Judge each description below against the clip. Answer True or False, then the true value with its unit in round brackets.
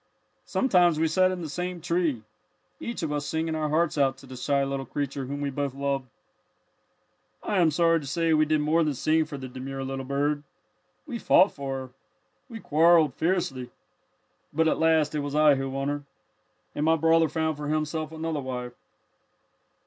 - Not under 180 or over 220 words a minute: True (185 wpm)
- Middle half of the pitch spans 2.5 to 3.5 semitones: True (2.9 semitones)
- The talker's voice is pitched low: False (150 Hz)